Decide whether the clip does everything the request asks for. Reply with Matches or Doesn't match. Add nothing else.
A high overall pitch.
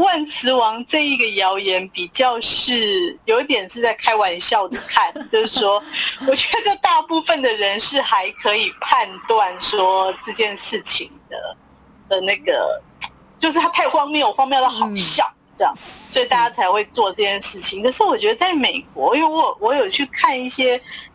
Matches